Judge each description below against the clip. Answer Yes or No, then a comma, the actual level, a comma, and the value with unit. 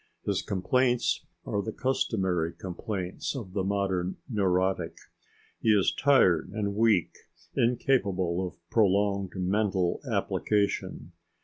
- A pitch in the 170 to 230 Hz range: No, low, 100 Hz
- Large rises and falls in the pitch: No, average, 3.0 semitones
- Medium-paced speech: No, slow, 105 wpm